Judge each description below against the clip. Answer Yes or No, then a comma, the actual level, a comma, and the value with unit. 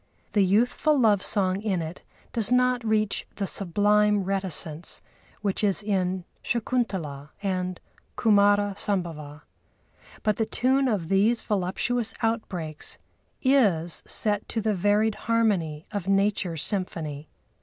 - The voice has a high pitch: Yes, high, 200 Hz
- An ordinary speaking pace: No, slow, 120 wpm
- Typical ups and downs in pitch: Yes, average, 3.3 semitones